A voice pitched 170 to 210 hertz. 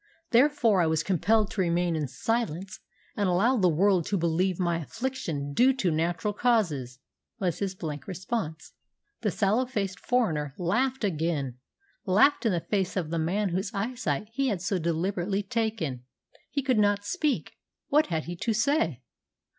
Yes: high, 190 Hz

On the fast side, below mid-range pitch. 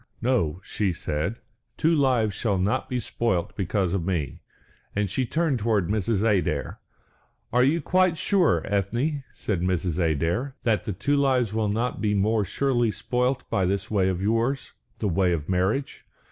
No: average, 165 wpm; low, 105 Hz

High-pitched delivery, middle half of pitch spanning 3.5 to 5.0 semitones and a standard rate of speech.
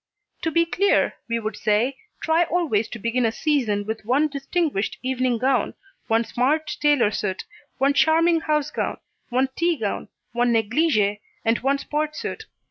No: very high, 260 Hz; wide, 5.4 semitones; average, 160 wpm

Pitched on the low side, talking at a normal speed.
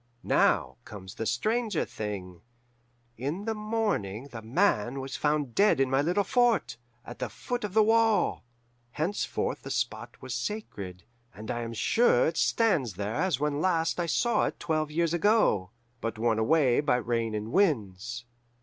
No: medium, 145 Hz; average, 165 wpm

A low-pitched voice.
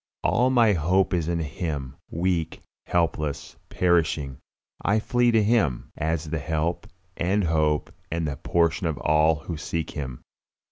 Yes: very low, 80 Hz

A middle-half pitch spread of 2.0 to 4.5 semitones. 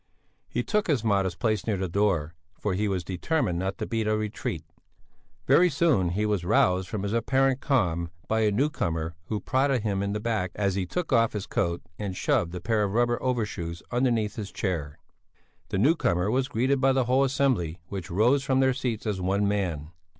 No: wide, 5.4 semitones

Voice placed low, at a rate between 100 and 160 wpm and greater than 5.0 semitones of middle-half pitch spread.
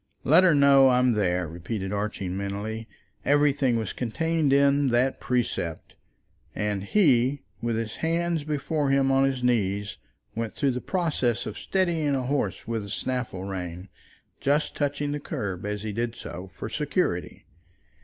Yes: low, 125 Hz; average, 155 wpm; wide, 5.6 semitones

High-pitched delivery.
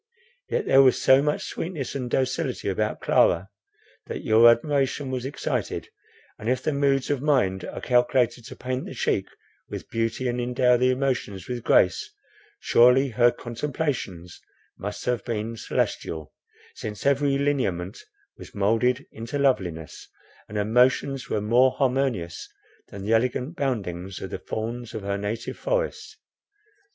No: low, 125 Hz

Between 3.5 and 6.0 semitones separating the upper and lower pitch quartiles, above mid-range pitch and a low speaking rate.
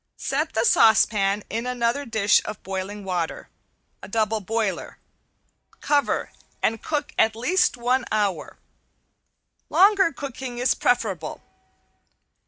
Yes: average, 4.2 semitones; high, 225 Hz; slow, 105 wpm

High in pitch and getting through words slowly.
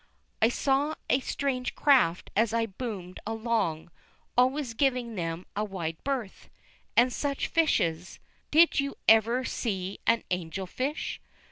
Yes: high, 230 Hz; slow, 125 wpm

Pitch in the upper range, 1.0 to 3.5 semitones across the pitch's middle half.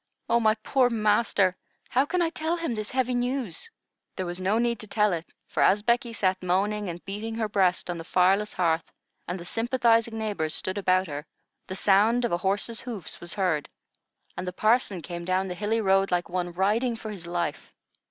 No: high, 205 Hz; average, 4.0 semitones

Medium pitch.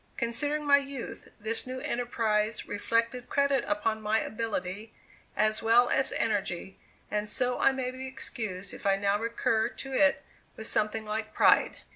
No: high, 225 Hz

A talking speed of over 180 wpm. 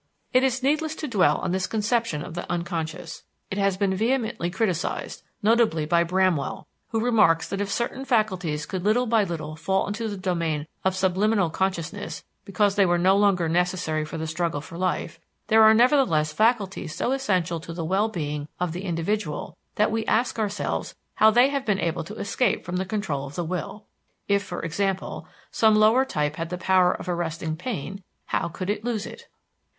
Yes: average, 190 wpm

